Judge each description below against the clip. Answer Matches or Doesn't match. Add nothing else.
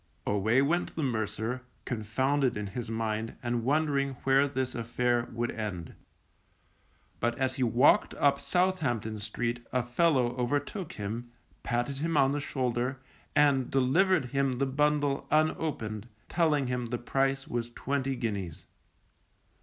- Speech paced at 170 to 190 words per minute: Doesn't match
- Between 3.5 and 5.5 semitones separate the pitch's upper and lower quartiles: Doesn't match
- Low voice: Matches